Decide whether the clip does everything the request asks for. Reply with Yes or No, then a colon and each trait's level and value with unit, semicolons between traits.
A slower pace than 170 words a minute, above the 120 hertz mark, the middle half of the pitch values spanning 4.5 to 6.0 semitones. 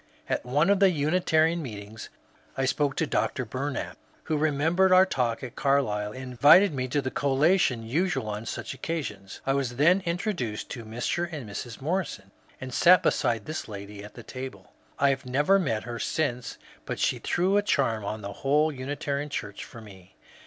No: average, 180 wpm; low, 135 Hz; wide, 5.6 semitones